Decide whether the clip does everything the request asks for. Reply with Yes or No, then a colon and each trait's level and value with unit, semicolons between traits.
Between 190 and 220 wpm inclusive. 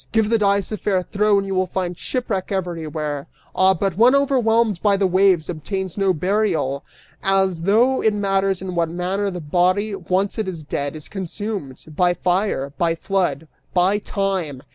No: average, 175 wpm